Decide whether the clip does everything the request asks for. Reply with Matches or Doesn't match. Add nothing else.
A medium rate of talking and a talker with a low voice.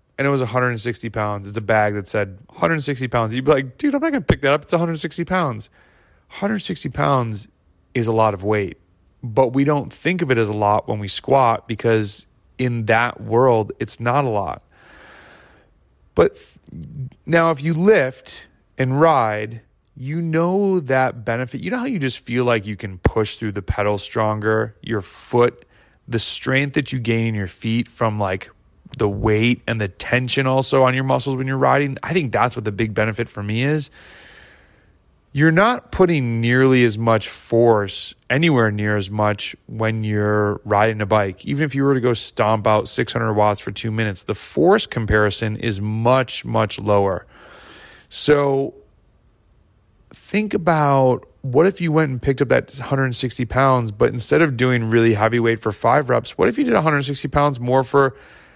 Matches